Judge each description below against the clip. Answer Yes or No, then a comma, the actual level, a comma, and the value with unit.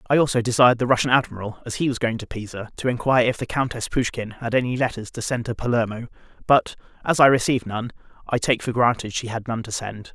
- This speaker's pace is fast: Yes, fast, 230 wpm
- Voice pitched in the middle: No, low, 120 Hz